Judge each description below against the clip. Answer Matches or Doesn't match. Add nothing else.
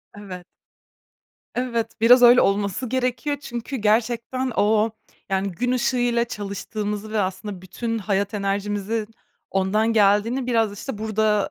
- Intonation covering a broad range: Doesn't match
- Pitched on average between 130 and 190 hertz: Doesn't match